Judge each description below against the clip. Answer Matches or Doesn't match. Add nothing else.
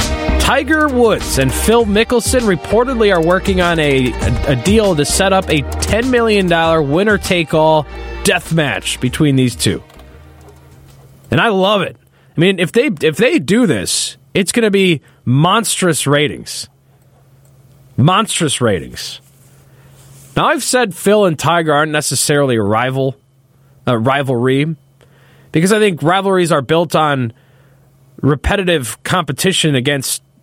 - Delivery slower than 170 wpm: Matches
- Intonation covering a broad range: Matches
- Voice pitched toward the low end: Doesn't match